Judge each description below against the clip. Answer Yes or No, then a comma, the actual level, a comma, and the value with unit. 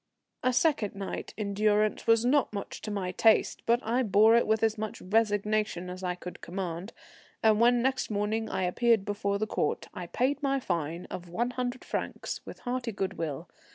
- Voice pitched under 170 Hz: No, high, 215 Hz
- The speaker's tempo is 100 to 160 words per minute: No, average, 190 wpm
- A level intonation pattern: No, average, 3.6 semitones